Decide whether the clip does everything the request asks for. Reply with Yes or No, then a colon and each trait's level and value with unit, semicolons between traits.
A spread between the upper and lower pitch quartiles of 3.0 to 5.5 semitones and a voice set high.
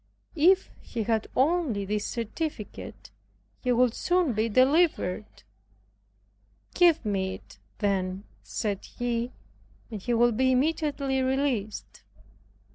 Yes: average, 5.2 semitones; high, 240 Hz